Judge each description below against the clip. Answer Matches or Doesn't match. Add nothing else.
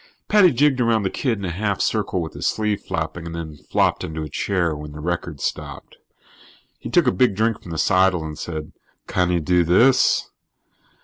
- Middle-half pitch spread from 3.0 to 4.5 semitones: Doesn't match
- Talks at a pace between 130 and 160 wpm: Doesn't match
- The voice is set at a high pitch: Doesn't match